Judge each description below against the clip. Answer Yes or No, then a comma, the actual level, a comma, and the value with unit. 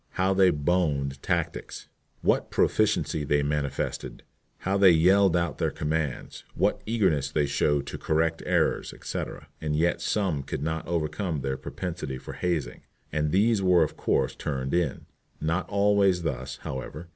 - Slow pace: No, average, 150 wpm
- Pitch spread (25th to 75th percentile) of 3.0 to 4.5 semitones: Yes, average, 4.1 semitones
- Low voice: Yes, very low, 80 Hz